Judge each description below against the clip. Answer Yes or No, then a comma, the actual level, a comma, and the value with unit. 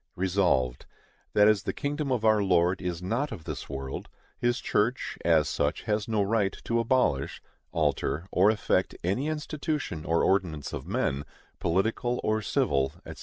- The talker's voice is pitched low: Yes, low, 100 Hz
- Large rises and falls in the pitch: Yes, wide, 5.8 semitones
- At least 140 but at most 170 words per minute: Yes, average, 160 wpm